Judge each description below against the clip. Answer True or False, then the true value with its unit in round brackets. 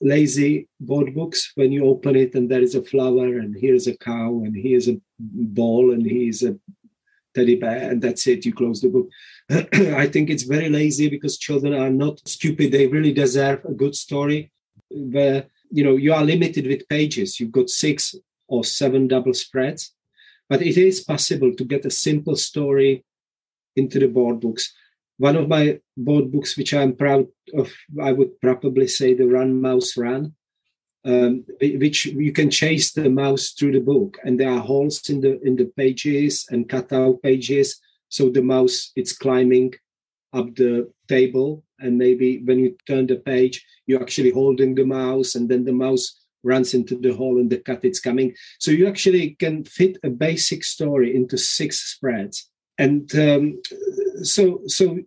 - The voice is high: False (135 Hz)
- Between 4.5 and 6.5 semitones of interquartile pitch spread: False (2.8 semitones)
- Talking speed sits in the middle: True (180 wpm)